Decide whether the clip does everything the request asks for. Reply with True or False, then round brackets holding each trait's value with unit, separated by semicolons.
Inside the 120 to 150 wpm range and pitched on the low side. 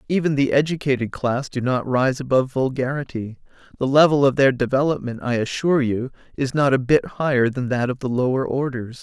False (185 wpm; 130 Hz)